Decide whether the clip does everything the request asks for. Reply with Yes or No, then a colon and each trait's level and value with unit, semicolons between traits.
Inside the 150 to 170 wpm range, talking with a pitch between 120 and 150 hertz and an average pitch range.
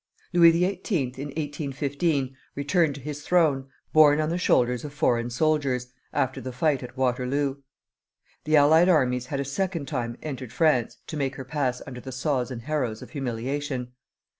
Yes: average, 165 wpm; medium, 140 Hz; average, 3.4 semitones